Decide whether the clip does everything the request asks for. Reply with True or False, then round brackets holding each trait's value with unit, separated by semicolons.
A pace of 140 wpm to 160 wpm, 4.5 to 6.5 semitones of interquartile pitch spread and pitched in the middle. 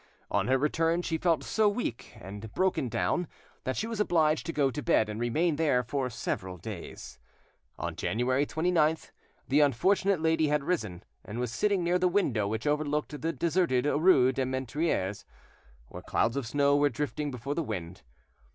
False (175 wpm; 5.4 semitones; 145 Hz)